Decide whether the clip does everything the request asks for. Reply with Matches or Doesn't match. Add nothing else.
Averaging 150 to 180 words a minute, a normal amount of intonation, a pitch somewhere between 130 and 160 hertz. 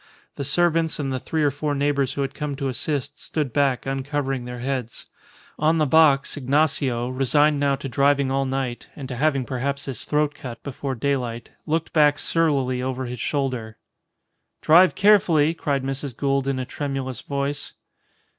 Doesn't match